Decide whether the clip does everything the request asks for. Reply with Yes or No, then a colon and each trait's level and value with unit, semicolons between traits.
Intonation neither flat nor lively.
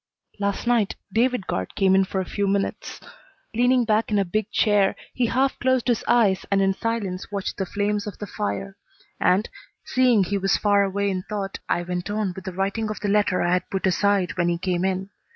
No: narrow, 2.2 semitones